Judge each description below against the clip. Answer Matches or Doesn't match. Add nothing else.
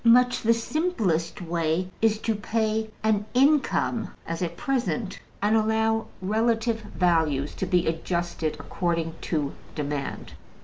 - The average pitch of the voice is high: Matches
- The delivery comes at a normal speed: Doesn't match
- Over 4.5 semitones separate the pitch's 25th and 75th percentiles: Matches